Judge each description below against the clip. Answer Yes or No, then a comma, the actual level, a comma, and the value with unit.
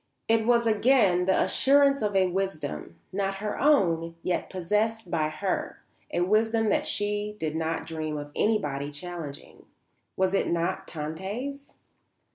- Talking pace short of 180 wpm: Yes, average, 140 wpm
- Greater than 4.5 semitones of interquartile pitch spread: Yes, average, 5.1 semitones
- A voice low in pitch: No, high, 190 Hz